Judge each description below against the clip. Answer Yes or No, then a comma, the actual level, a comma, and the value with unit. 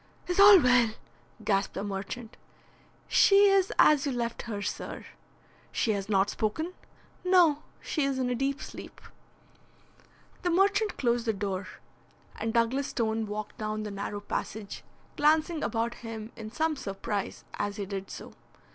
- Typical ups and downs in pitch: No, wide, 6.5 semitones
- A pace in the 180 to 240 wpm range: No, average, 150 wpm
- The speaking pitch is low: No, high, 230 Hz